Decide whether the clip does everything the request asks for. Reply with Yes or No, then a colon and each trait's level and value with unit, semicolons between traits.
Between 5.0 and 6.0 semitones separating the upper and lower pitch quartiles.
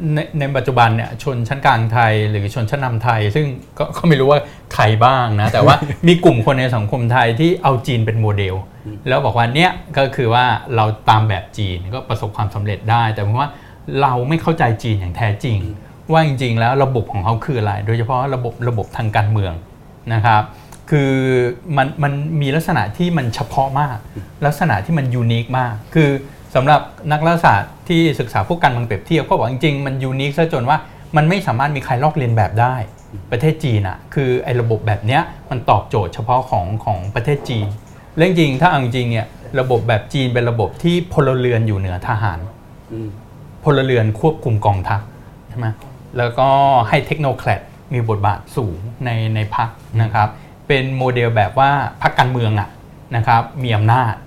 No: average, 4.2 semitones